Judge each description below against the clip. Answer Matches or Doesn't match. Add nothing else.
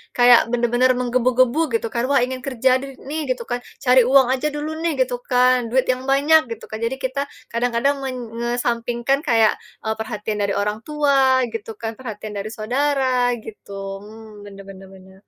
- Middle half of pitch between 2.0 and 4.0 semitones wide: Matches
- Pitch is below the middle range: Doesn't match